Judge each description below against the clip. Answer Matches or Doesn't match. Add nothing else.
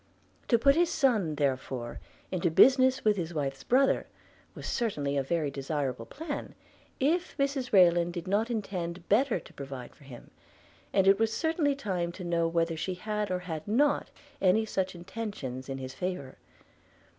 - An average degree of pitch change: Doesn't match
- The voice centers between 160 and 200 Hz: Matches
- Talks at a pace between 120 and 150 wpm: Doesn't match